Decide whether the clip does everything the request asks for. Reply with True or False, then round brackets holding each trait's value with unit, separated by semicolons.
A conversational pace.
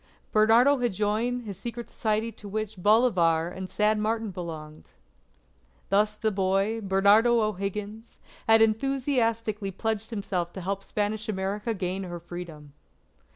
False (130 wpm)